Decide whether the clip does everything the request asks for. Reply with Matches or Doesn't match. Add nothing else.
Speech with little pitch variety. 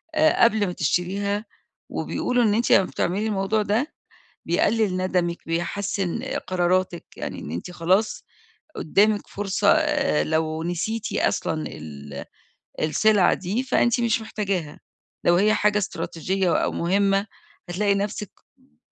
Doesn't match